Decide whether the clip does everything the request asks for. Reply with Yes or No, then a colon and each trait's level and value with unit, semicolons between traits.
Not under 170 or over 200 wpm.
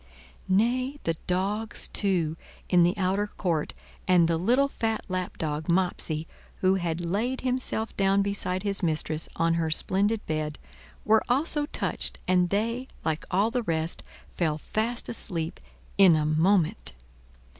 No: average, 140 wpm